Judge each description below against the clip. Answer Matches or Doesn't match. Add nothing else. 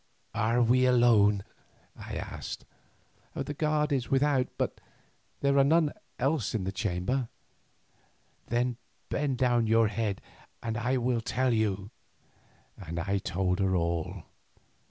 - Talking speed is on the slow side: Matches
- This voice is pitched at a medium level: Doesn't match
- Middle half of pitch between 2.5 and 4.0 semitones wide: Doesn't match